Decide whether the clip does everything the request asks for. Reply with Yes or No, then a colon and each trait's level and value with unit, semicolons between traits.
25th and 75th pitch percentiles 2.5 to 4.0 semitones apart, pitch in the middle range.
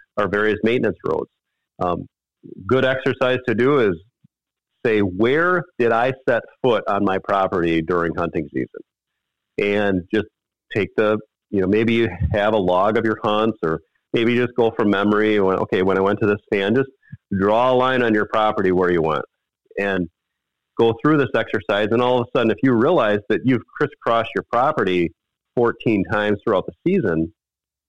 No: average, 3.3 semitones; low, 105 Hz